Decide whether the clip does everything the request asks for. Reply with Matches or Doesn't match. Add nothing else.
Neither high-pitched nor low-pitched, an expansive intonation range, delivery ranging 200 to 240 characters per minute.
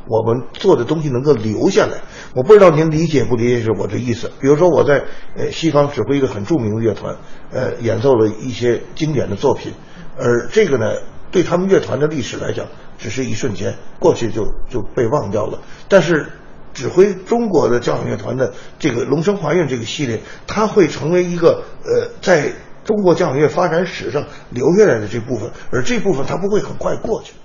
Doesn't match